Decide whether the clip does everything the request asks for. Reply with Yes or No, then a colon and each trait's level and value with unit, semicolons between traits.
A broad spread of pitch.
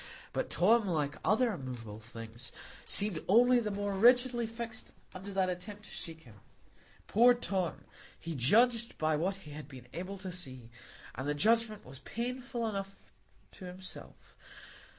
Yes: wide, 7.3 semitones